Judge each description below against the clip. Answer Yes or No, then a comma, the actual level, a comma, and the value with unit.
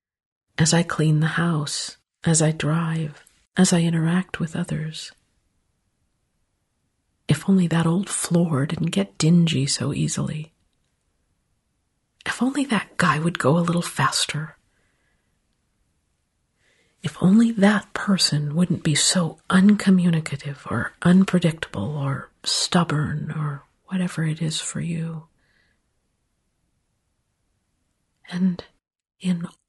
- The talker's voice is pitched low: No, medium, 165 Hz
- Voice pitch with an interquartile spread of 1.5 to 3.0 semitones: No, average, 3.4 semitones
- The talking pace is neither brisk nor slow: No, slow, 105 wpm